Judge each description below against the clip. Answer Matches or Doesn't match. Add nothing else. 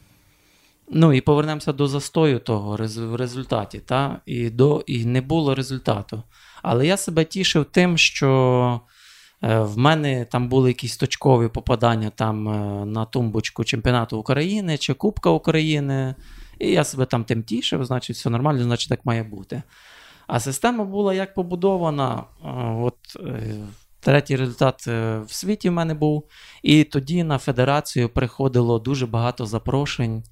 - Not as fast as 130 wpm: Doesn't match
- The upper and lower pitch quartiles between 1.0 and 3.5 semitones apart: Doesn't match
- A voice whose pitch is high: Doesn't match